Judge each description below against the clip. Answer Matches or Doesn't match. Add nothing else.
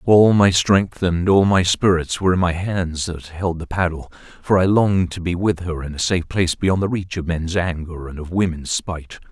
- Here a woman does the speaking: Doesn't match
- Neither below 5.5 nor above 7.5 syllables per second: Doesn't match